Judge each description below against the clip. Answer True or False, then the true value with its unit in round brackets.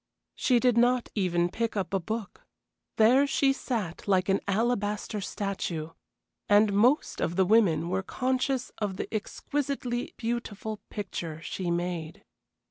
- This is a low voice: False (210 Hz)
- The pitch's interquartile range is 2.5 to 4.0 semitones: False (4.5 semitones)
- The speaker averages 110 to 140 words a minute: True (135 wpm)